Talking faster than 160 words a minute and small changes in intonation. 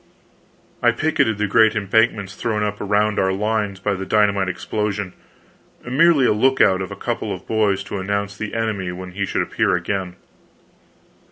Yes: average, 170 wpm; narrow, 2.3 semitones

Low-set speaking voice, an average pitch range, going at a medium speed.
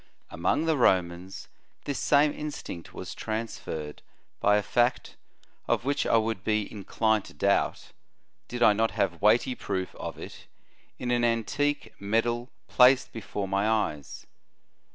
Yes: low, 110 Hz; average, 3.9 semitones; average, 150 wpm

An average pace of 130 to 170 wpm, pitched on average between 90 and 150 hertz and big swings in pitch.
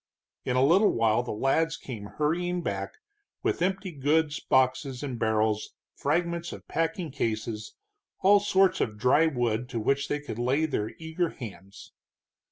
Yes: average, 155 wpm; low, 135 Hz; wide, 6.5 semitones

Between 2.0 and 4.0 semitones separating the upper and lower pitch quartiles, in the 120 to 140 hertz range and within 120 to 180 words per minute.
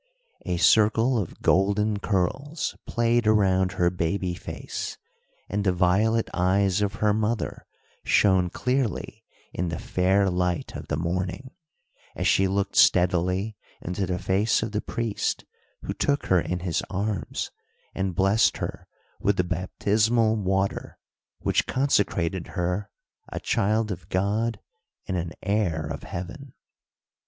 No: average, 3.1 semitones; very low, 95 Hz; slow, 135 wpm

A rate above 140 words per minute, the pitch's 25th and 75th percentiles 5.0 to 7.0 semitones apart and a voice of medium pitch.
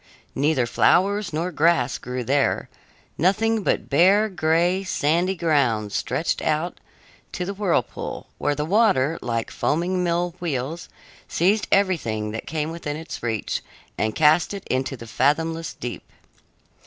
No: slow, 135 wpm; average, 5.3 semitones; medium, 160 Hz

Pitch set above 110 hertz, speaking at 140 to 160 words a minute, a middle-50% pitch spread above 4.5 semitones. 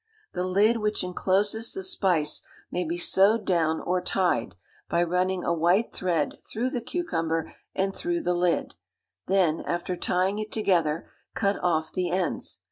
No: medium, 185 Hz; average, 155 wpm; average, 3.2 semitones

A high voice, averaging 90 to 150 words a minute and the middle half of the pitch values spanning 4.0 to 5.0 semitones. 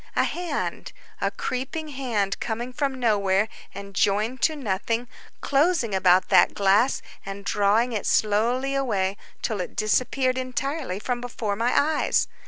Yes: high, 235 Hz; average, 140 wpm; average, 4.7 semitones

